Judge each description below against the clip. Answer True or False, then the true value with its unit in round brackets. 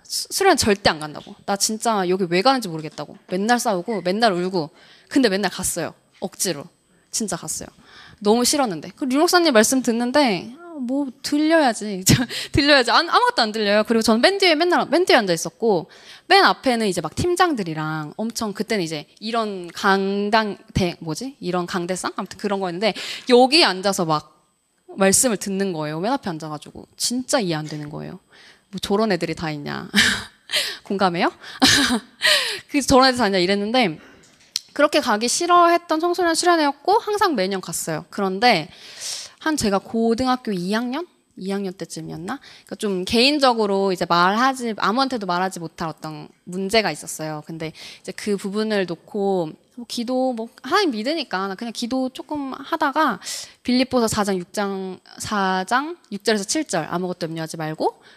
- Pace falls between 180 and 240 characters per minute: False (335 characters per minute)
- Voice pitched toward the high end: True (210 Hz)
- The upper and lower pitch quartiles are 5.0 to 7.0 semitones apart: True (6.3 semitones)